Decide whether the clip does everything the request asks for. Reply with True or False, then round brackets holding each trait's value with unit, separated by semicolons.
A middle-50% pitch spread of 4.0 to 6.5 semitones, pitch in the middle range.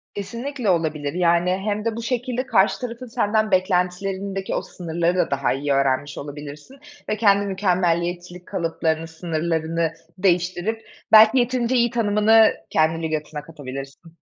True (5.0 semitones; 180 Hz)